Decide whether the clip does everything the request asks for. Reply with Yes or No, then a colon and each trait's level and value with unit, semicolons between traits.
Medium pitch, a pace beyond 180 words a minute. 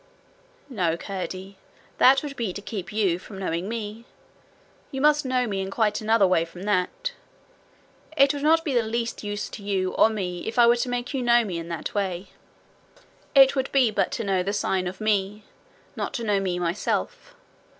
No: high, 210 Hz; average, 200 wpm